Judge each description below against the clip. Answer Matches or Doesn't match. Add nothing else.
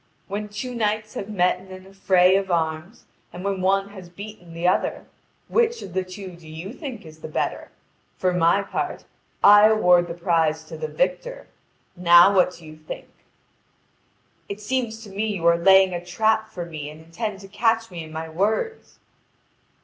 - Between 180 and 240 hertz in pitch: Matches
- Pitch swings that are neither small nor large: Matches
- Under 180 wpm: Doesn't match